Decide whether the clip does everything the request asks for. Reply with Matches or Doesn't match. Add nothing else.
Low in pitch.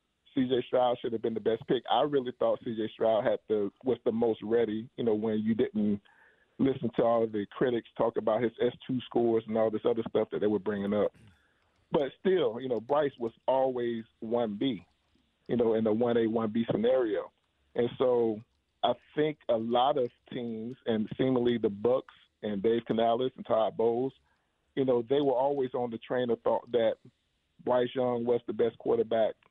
Matches